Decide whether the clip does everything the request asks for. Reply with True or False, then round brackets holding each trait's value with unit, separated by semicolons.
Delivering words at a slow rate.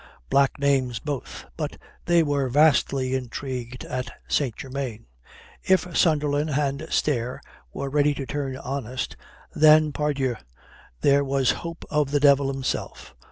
True (130 wpm)